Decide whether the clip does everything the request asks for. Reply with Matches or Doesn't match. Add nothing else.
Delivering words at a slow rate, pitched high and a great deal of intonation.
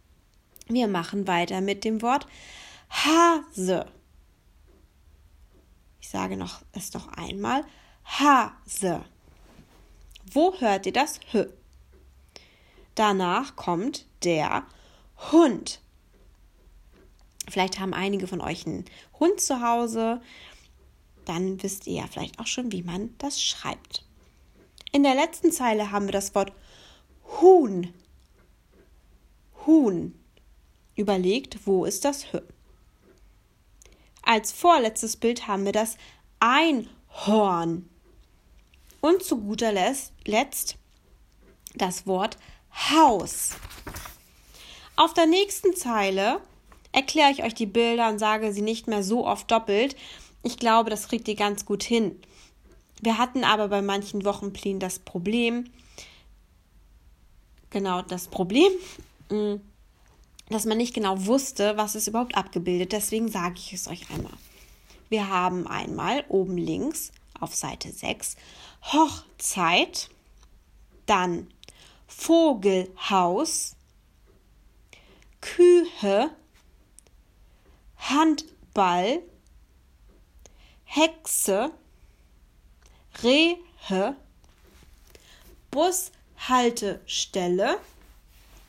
Matches